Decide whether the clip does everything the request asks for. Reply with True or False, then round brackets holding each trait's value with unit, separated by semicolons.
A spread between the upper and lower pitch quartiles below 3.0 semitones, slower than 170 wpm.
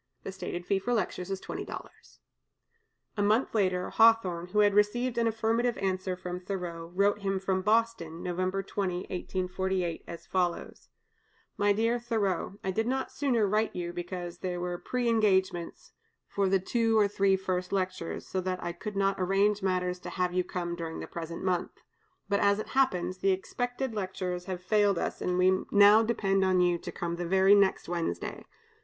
False (2.6 semitones; 180 wpm)